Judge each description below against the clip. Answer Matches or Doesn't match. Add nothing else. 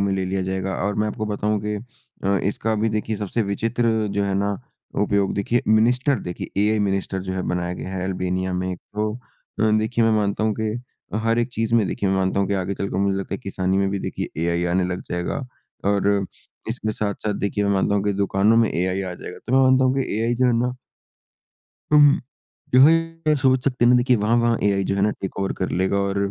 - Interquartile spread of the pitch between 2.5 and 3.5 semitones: Matches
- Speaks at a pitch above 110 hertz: Doesn't match